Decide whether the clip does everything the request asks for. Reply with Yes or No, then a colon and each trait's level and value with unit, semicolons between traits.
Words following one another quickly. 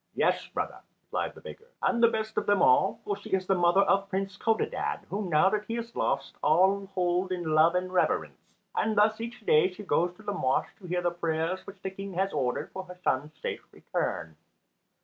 Yes: fast, 215 wpm